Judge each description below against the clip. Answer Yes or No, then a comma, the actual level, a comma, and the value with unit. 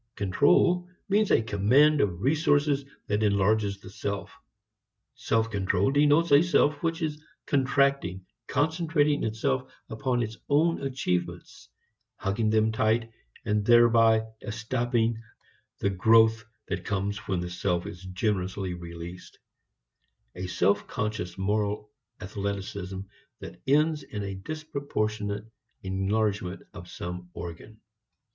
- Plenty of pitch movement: Yes, wide, 6.1 semitones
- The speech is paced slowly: Yes, slow, 115 wpm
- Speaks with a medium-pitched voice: No, low, 110 Hz